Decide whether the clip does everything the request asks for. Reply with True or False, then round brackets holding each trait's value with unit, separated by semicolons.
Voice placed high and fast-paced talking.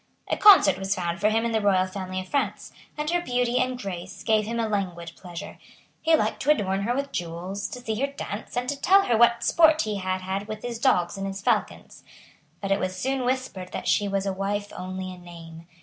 True (205 Hz; 230 wpm)